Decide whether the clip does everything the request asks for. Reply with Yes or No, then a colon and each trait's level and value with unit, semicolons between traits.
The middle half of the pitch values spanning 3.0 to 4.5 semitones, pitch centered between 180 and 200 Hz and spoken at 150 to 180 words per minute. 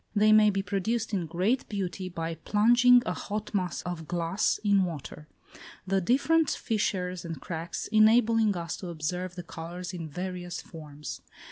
Yes: average, 3.9 semitones; medium, 185 Hz; average, 155 wpm